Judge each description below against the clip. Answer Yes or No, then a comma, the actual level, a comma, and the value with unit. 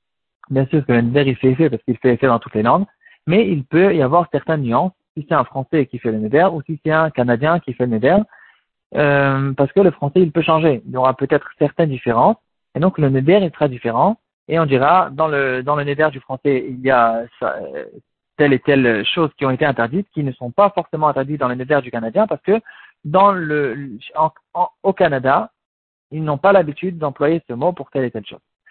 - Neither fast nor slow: No, fast, 230 wpm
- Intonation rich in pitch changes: No, average, 4.2 semitones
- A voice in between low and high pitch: Yes, medium, 145 Hz